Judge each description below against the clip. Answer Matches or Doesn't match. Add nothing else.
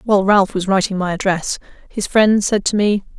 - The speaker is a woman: Matches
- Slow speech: Doesn't match